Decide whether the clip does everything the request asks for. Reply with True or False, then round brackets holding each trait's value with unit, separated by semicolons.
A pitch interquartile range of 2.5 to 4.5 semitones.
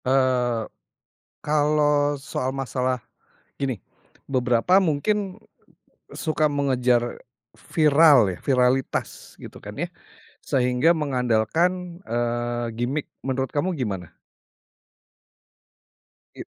True (3.6 semitones)